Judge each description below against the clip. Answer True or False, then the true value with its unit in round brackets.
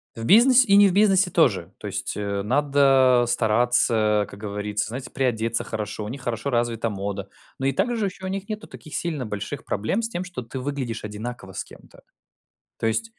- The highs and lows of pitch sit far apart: True (8.3 semitones)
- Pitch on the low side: True (120 Hz)